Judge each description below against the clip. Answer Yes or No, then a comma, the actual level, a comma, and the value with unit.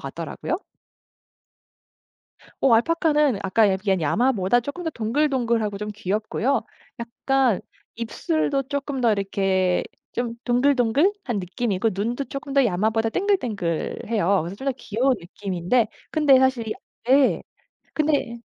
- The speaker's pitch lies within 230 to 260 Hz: Yes, high, 235 Hz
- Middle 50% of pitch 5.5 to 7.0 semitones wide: No, average, 5.1 semitones